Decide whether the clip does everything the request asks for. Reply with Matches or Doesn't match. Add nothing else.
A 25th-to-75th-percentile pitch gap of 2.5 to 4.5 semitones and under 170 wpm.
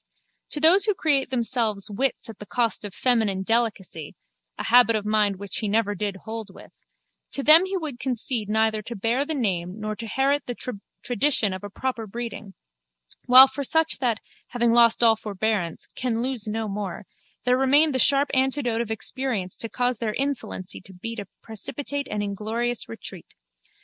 Doesn't match